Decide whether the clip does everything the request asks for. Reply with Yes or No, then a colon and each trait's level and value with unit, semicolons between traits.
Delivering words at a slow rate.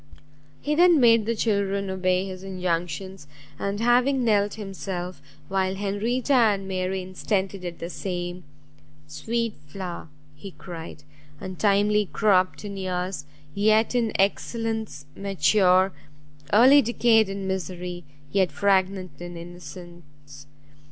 Yes: slow, 115 wpm